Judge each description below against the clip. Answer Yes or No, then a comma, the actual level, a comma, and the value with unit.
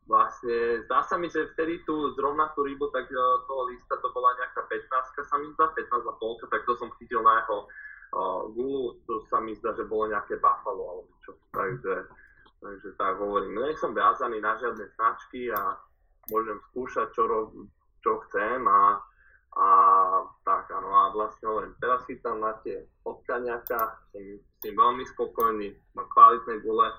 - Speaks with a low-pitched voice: No, very high, 370 Hz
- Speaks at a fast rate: Yes, fast, 175 wpm